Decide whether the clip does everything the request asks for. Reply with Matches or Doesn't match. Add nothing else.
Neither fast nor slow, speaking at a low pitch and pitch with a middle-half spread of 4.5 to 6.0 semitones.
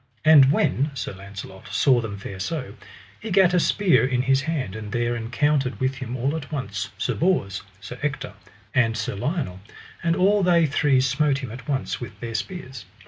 Matches